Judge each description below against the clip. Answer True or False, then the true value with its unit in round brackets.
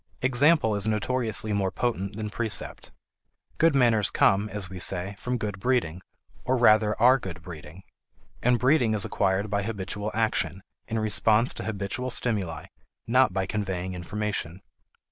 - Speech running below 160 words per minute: True (145 wpm)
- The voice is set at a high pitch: False (105 Hz)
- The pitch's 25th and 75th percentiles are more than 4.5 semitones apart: False (3.6 semitones)